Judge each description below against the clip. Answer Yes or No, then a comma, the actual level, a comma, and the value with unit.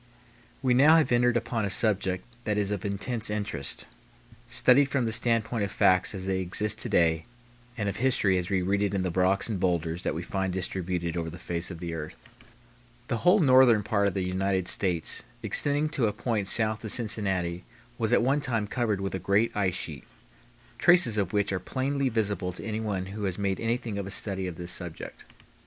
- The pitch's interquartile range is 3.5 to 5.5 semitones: Yes, average, 3.8 semitones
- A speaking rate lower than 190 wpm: No, fast, 205 wpm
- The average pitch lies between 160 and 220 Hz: No, low, 100 Hz